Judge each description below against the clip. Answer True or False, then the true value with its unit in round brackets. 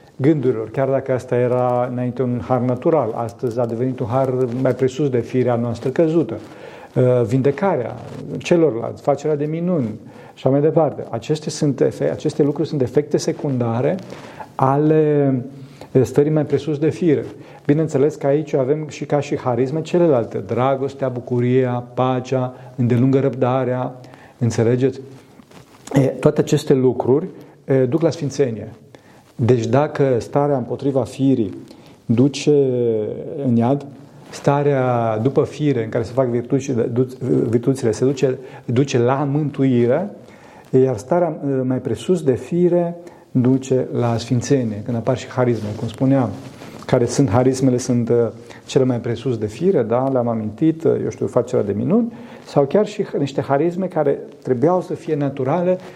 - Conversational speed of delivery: True (140 wpm)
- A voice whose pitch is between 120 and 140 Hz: True (135 Hz)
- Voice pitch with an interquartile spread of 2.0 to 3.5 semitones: True (3.1 semitones)